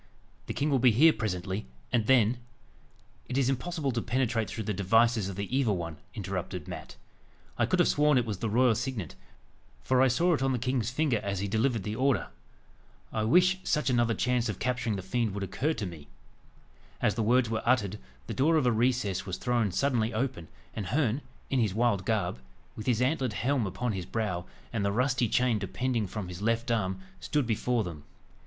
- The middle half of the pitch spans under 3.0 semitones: No, average, 4.1 semitones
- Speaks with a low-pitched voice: Yes, low, 115 Hz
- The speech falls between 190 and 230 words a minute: Yes, fast, 205 wpm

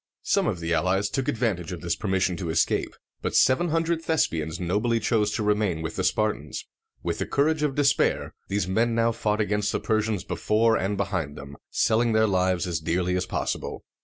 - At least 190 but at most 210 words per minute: Yes, average, 195 wpm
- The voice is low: Yes, low, 105 Hz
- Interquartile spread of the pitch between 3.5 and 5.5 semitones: Yes, average, 4.2 semitones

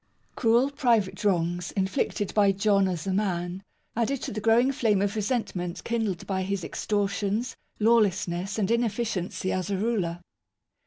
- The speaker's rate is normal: Yes, average, 150 wpm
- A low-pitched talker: No, high, 200 Hz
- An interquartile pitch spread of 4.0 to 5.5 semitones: No, average, 3.2 semitones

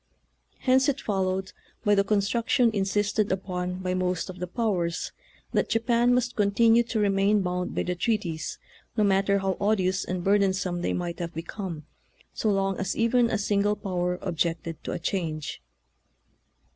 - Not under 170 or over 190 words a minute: No, average, 160 wpm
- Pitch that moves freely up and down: No, average, 2.9 semitones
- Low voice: No, high, 195 Hz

